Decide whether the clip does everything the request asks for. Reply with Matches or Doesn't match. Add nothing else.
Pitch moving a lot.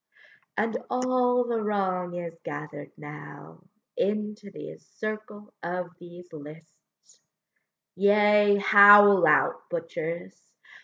Doesn't match